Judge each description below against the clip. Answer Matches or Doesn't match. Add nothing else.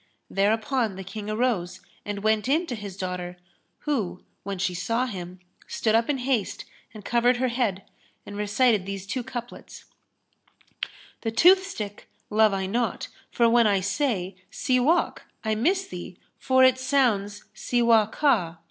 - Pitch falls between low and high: Doesn't match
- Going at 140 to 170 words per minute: Matches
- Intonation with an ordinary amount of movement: Matches